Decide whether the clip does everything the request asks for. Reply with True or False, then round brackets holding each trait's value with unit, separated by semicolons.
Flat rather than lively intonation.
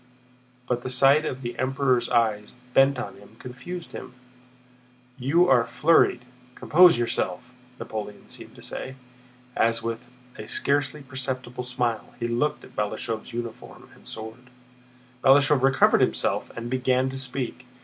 True (2.2 semitones)